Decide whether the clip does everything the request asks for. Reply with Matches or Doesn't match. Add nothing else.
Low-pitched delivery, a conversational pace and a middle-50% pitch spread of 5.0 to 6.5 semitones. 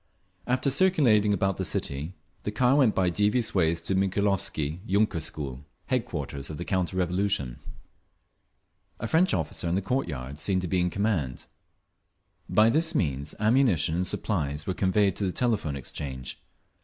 Matches